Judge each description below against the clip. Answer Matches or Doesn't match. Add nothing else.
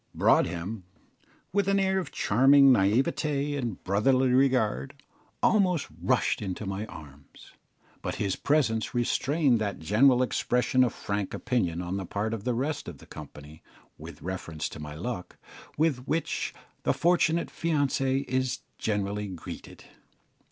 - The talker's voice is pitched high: Doesn't match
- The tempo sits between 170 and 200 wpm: Doesn't match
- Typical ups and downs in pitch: Doesn't match